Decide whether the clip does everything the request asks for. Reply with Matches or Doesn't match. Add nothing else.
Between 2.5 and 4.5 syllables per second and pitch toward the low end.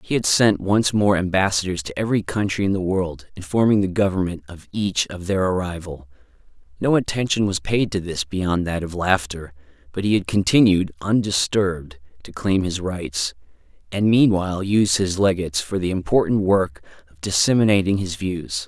Doesn't match